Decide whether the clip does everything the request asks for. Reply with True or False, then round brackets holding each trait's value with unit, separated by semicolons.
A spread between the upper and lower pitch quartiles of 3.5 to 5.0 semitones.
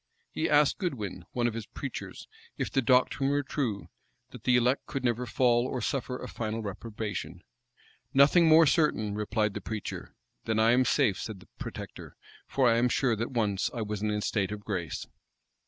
True (3.8 semitones)